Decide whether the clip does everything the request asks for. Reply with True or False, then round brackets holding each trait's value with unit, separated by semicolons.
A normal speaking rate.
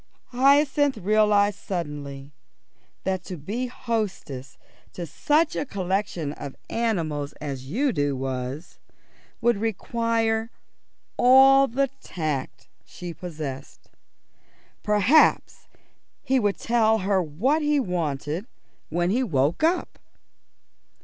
False (100 wpm)